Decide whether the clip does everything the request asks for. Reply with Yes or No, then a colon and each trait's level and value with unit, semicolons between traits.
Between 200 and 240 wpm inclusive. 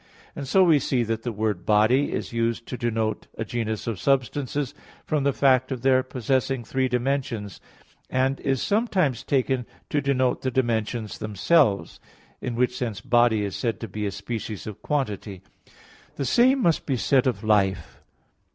No: average, 170 wpm